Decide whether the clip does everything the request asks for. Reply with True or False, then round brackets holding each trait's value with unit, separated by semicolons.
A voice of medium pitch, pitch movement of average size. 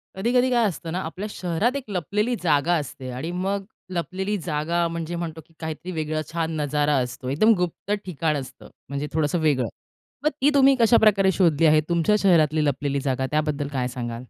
True (165 Hz; 4.4 semitones)